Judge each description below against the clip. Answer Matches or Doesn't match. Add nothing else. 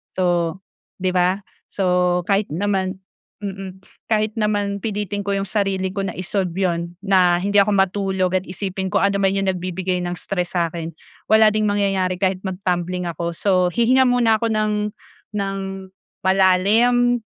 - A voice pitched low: Doesn't match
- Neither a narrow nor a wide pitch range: Doesn't match